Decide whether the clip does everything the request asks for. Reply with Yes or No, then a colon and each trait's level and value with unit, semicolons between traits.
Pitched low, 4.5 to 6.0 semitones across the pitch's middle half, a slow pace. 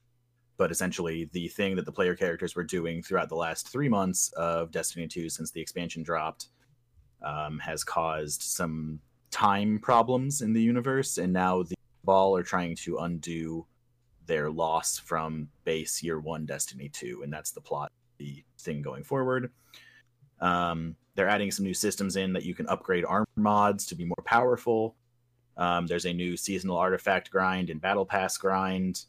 No: very low, 90 Hz; average, 5.3 semitones; average, 170 wpm